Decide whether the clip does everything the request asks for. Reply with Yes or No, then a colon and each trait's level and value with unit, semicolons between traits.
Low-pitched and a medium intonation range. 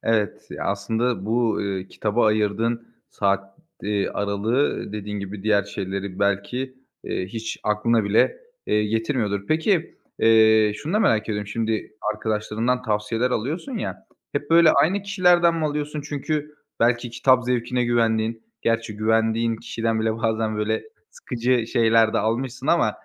Yes: low, 115 Hz; average, 3.0 semitones